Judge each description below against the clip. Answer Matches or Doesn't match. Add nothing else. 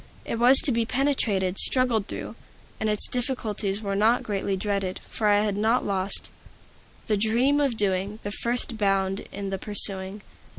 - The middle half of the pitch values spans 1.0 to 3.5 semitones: Matches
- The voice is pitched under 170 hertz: Doesn't match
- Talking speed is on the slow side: Doesn't match